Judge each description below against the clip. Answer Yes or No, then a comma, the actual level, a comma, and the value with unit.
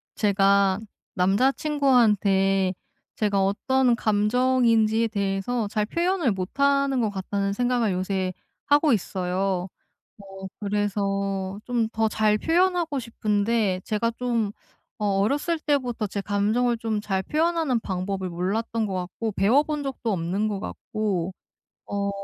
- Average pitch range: Yes, average, 4.1 semitones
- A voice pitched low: No, high, 210 Hz